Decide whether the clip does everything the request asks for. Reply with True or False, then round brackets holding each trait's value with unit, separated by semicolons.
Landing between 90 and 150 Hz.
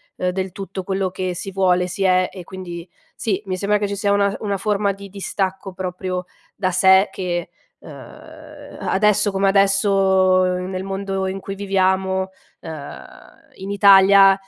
False (190 Hz)